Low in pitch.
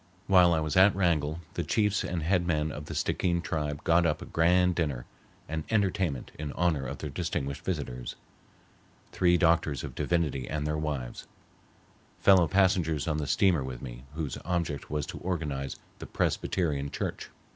Yes: very low, 80 Hz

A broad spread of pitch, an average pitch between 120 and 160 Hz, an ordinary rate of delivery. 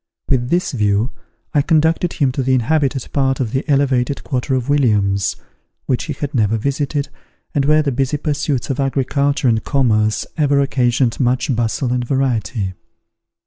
No: average, 2.9 semitones; low, 135 Hz; average, 160 wpm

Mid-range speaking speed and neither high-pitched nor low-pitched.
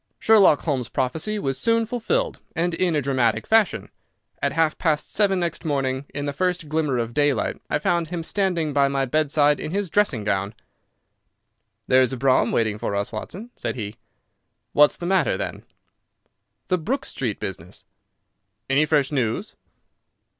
Yes: average, 160 wpm; medium, 150 Hz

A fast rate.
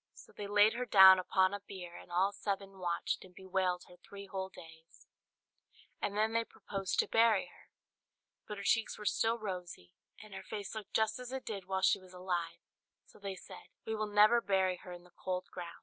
Yes: fast, 210 wpm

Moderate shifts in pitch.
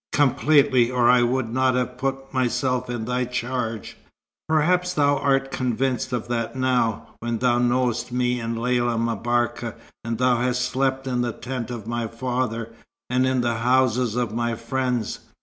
No: narrow, 1.7 semitones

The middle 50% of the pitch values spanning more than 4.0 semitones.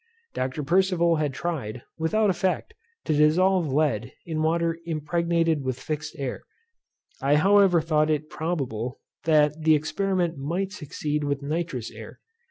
No: average, 2.9 semitones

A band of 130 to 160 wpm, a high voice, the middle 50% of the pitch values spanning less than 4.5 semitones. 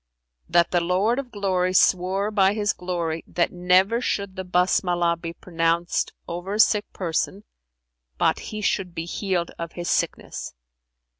No: average, 150 wpm; medium, 180 Hz; narrow, 2.6 semitones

